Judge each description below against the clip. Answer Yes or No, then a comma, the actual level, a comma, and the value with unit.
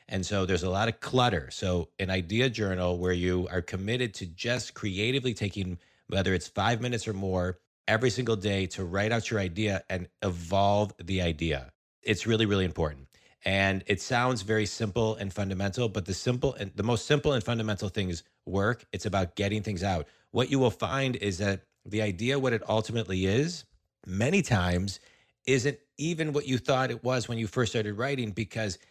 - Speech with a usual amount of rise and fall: Yes, average, 4.1 semitones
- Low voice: Yes, low, 105 Hz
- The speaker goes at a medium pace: Yes, average, 190 wpm